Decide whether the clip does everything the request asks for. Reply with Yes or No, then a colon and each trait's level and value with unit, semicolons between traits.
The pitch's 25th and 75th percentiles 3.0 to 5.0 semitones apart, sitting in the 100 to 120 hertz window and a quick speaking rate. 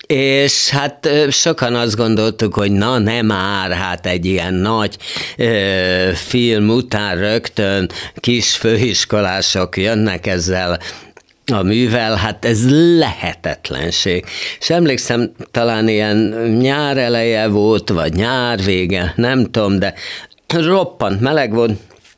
No: average, 3.9 semitones; low, 110 Hz; average, 115 wpm